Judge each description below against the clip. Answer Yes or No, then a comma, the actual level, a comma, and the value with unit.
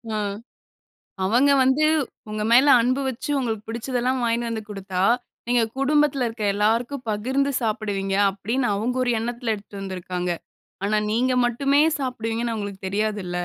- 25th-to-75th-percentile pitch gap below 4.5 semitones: Yes, average, 3.7 semitones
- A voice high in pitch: Yes, high, 230 Hz